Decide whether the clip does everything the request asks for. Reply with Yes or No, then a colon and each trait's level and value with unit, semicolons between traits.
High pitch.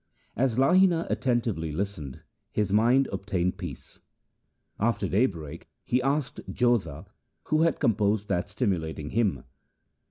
No: low, 105 Hz